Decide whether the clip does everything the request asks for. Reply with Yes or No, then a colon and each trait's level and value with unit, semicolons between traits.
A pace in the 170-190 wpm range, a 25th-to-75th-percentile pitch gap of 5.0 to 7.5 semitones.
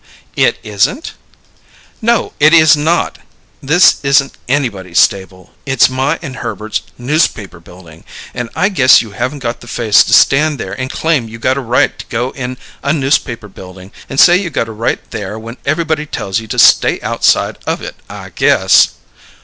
Yes: average, 175 wpm; wide, 5.6 semitones